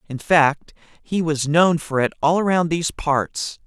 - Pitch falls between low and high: Yes, medium, 160 Hz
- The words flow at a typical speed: Yes, average, 180 wpm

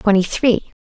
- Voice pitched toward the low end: No, high, 210 Hz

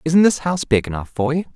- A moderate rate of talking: No, fast, 270 wpm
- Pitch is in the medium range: Yes, medium, 145 Hz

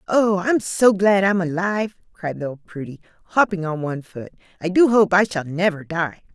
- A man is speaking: No, female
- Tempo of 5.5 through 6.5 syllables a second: No, 5.3 syllables/s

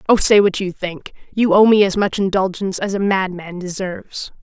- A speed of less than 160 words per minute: No, fast, 205 wpm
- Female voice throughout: Yes, female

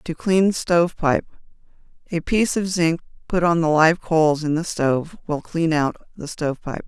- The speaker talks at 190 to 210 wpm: No, average, 165 wpm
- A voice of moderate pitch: Yes, medium, 165 Hz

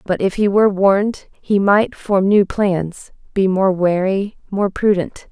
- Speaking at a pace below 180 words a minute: Yes, average, 170 wpm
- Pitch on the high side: Yes, high, 195 Hz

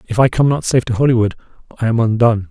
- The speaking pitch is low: Yes, low, 115 Hz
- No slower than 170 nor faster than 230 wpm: No, fast, 240 wpm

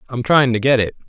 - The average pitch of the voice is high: No, low, 125 Hz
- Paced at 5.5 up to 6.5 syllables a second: Yes, 6.2 syllables/s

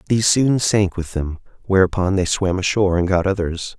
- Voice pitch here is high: No, very low, 95 Hz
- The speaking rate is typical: Yes, average, 190 wpm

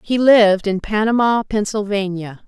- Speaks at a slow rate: Yes, slow, 120 wpm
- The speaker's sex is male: No, female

